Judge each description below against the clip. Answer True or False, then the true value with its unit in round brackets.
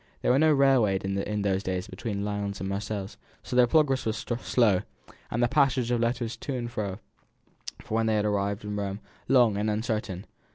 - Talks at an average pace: True (190 wpm)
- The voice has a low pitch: True (110 Hz)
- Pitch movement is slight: False (3.3 semitones)